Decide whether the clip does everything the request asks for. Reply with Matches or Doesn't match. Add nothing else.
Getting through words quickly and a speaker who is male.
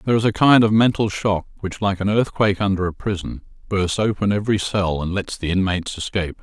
Matches